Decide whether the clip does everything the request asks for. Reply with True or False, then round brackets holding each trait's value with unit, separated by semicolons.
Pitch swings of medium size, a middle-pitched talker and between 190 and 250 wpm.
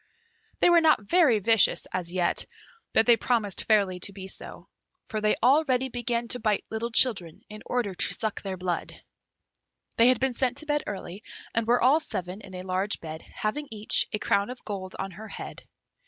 False (4.5 semitones; 215 Hz; 195 wpm)